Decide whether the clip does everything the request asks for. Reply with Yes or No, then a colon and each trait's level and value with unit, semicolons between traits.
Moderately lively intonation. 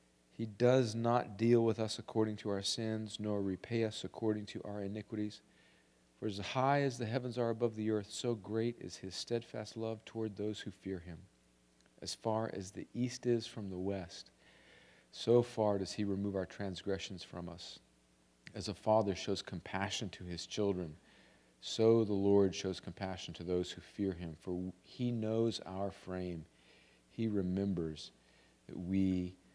Yes: average, 3.7 semitones